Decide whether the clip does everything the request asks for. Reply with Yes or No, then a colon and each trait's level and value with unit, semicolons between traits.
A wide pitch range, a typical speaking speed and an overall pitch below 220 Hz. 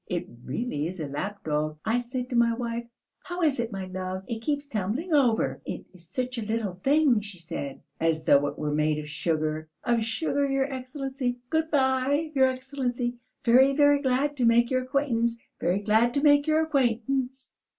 No: wide, 6.2 semitones; average, 185 wpm; high, 240 Hz